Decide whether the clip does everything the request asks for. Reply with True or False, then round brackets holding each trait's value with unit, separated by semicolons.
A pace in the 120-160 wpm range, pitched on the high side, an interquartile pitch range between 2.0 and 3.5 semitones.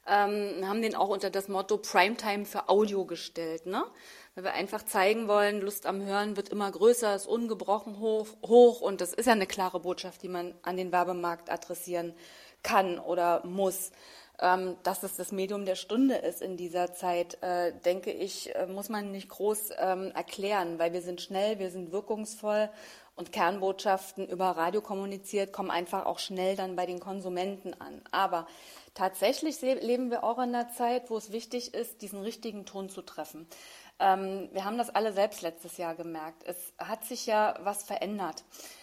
False (175 wpm; 195 Hz; 2.9 semitones)